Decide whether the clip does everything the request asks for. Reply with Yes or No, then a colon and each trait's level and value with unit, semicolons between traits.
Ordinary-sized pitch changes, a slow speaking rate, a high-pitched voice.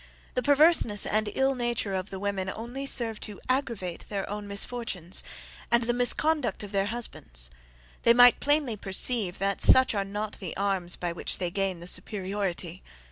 No: average, 4.1 semitones; average, 170 wpm; high, 205 Hz